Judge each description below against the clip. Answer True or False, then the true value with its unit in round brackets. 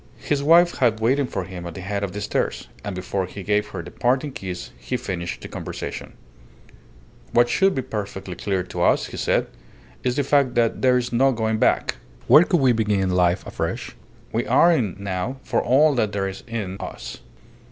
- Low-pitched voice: True (105 Hz)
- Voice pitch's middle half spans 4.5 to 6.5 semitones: True (5.5 semitones)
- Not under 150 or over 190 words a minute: False (200 wpm)